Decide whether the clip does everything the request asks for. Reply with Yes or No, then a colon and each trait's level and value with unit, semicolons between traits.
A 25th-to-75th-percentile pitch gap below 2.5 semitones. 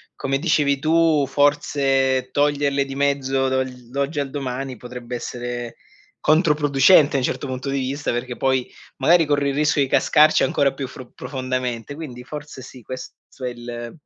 Yes: narrow, 2.1 semitones